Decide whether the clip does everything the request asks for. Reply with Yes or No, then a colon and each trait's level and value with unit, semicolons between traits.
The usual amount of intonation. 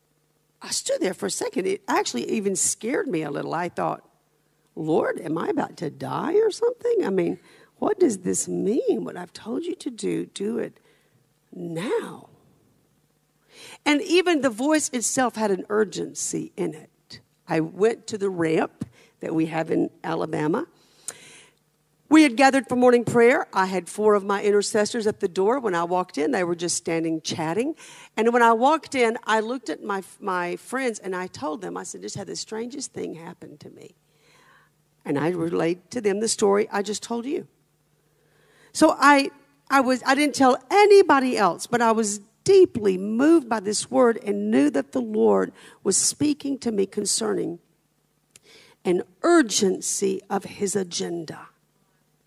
No: wide, 6.5 semitones